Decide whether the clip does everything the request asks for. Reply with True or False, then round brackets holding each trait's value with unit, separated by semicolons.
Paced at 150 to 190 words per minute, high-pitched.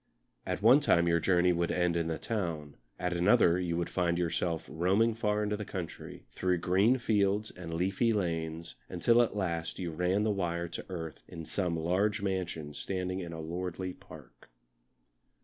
False (175 wpm; 90 Hz)